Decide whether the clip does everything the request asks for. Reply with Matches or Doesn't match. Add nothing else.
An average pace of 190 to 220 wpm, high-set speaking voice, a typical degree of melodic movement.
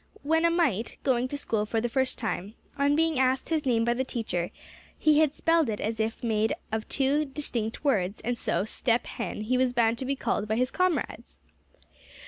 Matches